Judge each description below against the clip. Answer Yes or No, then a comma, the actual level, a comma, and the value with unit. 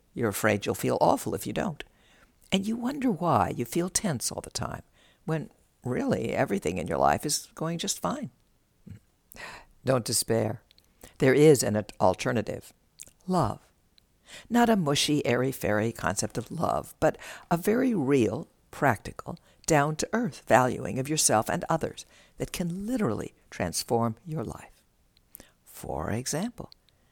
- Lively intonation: Yes, wide, 8.3 semitones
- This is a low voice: No, medium, 145 Hz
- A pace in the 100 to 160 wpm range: Yes, average, 140 wpm